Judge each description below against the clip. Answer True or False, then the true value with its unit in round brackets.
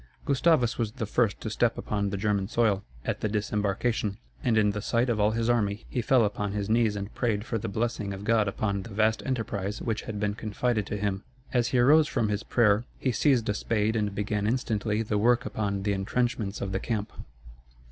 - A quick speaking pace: True (215 wpm)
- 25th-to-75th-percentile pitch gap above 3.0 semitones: False (2.4 semitones)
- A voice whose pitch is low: True (110 Hz)